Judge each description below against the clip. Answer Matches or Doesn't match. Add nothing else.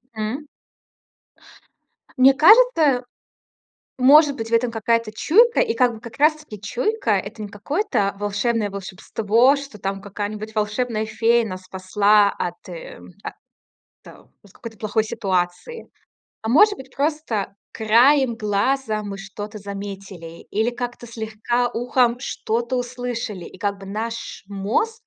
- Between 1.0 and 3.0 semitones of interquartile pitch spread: Doesn't match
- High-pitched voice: Matches